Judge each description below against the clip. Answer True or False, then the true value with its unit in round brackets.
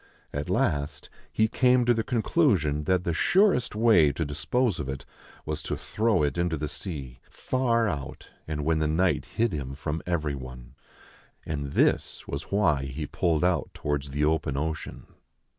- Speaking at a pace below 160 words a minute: False (170 wpm)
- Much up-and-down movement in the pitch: True (6.5 semitones)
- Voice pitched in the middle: False (80 Hz)